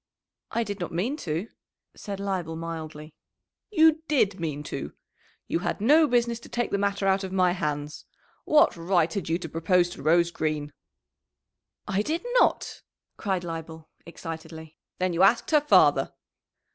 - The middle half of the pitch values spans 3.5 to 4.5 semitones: Yes, average, 4.0 semitones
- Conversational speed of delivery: Yes, average, 160 wpm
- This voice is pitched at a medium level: Yes, medium, 180 Hz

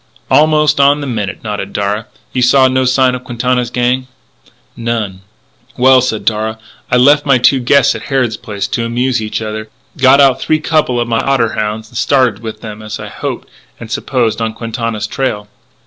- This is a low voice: Yes, low, 120 Hz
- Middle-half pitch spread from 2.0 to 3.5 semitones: Yes, average, 3.0 semitones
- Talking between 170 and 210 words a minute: Yes, average, 180 wpm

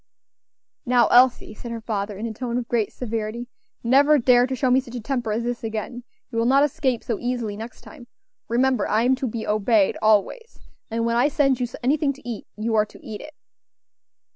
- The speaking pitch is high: Yes, high, 240 Hz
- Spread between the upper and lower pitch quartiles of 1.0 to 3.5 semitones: Yes, narrow, 2.6 semitones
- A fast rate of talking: Yes, fast, 210 wpm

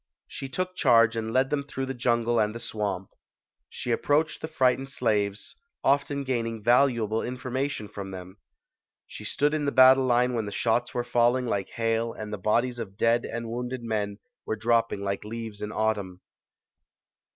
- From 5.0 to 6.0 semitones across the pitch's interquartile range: No, average, 3.2 semitones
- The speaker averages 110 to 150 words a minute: No, average, 175 wpm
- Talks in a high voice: No, low, 115 Hz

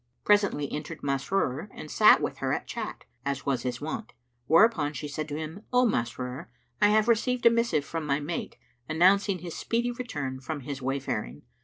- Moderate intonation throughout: No, wide, 6.9 semitones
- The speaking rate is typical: Yes, average, 180 wpm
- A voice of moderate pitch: Yes, medium, 155 Hz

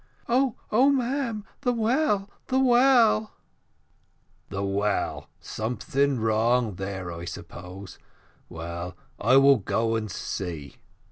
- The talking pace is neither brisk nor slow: No, slow, 115 wpm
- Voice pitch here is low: Yes, low, 120 Hz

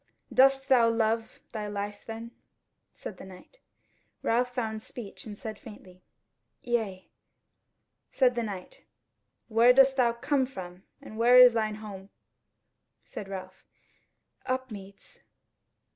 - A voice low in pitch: No, high, 225 Hz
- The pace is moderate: No, slow, 115 wpm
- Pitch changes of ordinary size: Yes, average, 3.5 semitones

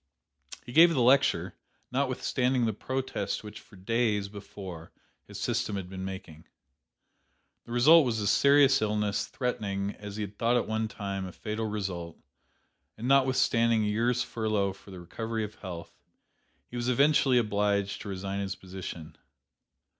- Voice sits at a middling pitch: No, low, 105 Hz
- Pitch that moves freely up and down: No, average, 3.8 semitones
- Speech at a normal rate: Yes, average, 150 wpm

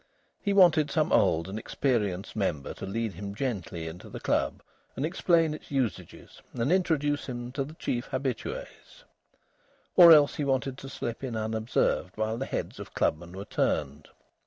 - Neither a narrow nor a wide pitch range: No, wide, 6.4 semitones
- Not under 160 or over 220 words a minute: Yes, average, 165 wpm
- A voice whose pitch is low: Yes, low, 120 Hz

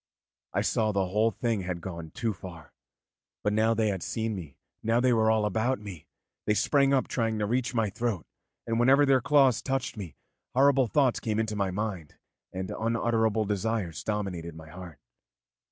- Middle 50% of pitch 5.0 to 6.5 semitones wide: No, average, 3.8 semitones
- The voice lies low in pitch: Yes, low, 110 Hz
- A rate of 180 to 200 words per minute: Yes, average, 185 wpm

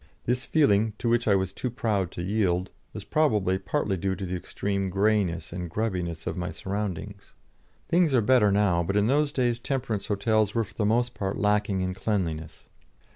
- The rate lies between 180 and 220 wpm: Yes, average, 185 wpm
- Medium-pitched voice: No, low, 100 Hz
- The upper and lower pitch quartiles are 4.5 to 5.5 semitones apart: No, average, 3.3 semitones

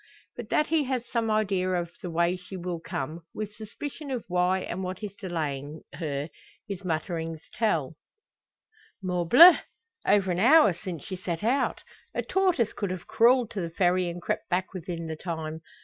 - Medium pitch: Yes, medium, 180 Hz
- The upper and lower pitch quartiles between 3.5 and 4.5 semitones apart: Yes, average, 4.2 semitones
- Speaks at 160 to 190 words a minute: Yes, average, 175 wpm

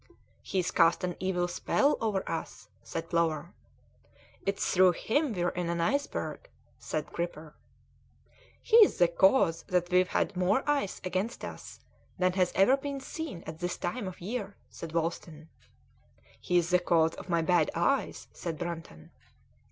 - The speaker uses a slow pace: No, average, 150 wpm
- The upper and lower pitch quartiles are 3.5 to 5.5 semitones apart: No, average, 2.8 semitones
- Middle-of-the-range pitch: Yes, medium, 180 Hz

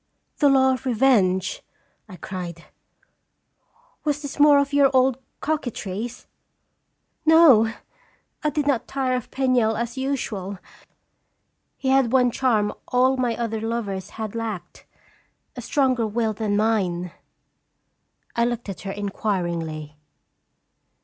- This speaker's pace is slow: Yes, slow, 125 wpm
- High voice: Yes, high, 235 Hz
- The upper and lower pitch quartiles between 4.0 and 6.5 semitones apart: Yes, average, 4.6 semitones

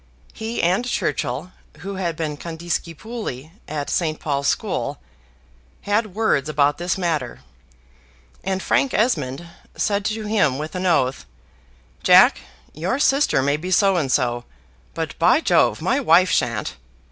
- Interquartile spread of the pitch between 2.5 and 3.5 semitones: No, wide, 5.6 semitones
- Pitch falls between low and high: Yes, medium, 170 Hz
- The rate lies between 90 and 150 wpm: Yes, slow, 135 wpm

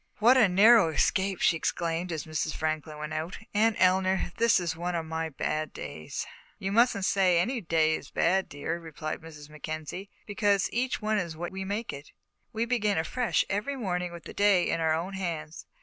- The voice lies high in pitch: No, medium, 180 Hz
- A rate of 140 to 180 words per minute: No, average, 195 wpm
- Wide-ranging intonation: No, average, 4.2 semitones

